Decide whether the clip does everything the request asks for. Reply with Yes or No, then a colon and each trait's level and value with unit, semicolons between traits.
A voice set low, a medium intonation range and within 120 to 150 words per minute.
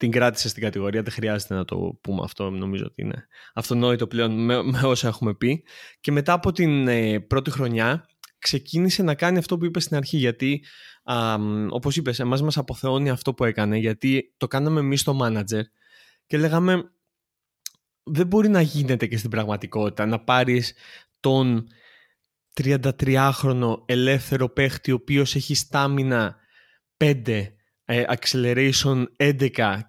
Yes: low, 130 Hz; average, 3.7 semitones; average, 145 wpm